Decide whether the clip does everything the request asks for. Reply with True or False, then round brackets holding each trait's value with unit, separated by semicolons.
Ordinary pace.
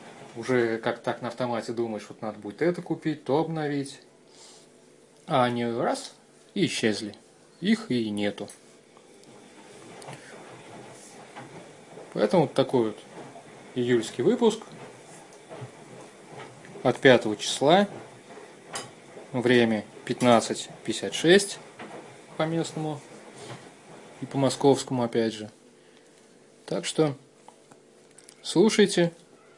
False (85 wpm)